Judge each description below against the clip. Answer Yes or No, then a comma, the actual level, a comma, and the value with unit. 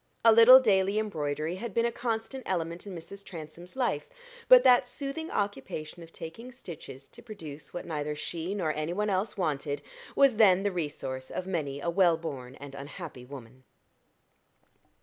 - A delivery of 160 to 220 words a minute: Yes, average, 170 wpm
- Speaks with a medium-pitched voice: Yes, medium, 175 Hz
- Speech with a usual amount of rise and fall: No, wide, 6.2 semitones